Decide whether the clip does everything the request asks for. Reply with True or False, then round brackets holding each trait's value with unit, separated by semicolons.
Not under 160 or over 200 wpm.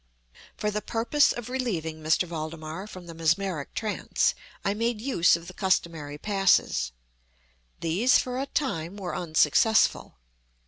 False (135 wpm)